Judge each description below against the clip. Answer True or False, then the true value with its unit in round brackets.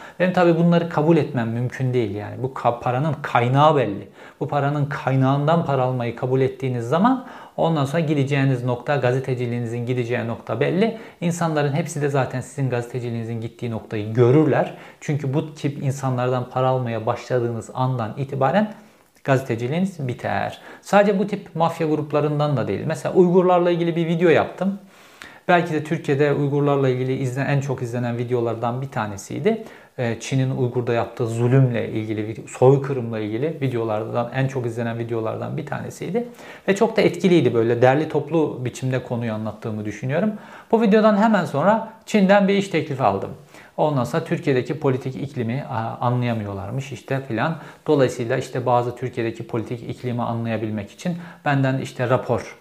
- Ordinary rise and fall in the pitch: True (4.8 semitones)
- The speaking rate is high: True (145 wpm)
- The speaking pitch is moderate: False (130 Hz)